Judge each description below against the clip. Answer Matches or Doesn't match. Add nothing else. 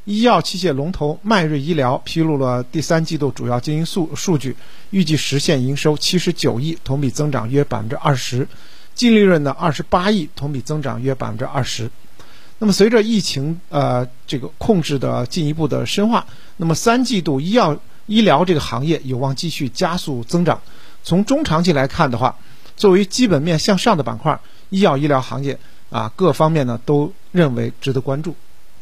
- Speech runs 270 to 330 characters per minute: Matches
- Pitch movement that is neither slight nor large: Matches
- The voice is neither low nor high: Matches